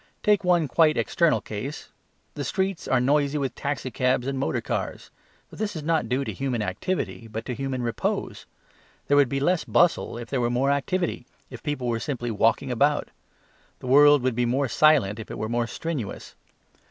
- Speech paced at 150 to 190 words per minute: Yes, average, 185 wpm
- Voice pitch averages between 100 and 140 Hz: Yes, low, 135 Hz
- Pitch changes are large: No, average, 3.7 semitones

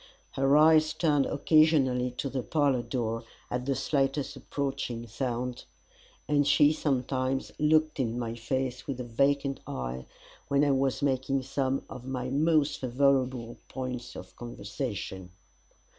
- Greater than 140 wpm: No, slow, 135 wpm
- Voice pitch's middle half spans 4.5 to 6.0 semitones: No, narrow, 2.5 semitones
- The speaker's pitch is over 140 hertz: No, low, 135 Hz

